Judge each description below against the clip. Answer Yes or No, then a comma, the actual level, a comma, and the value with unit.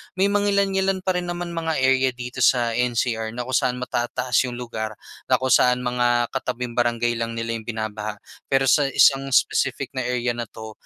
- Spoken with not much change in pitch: Yes, narrow, 2.3 semitones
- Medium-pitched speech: No, low, 125 Hz